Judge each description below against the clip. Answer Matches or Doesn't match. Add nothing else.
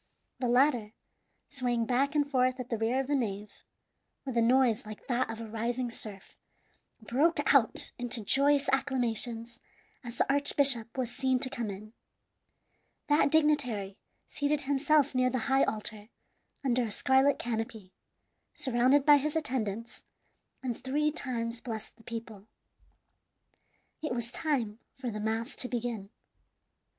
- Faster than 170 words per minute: Doesn't match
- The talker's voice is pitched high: Matches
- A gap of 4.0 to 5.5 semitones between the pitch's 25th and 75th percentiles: Doesn't match